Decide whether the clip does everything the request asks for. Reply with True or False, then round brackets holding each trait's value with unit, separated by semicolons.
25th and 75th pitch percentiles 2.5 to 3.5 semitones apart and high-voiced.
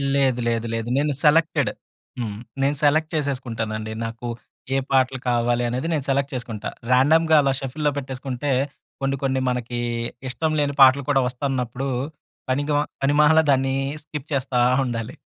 False (2.9 semitones; 135 Hz)